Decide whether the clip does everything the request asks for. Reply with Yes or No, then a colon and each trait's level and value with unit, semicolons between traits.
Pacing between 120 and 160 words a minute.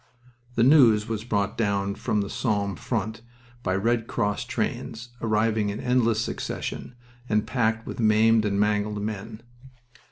Yes: average, 140 wpm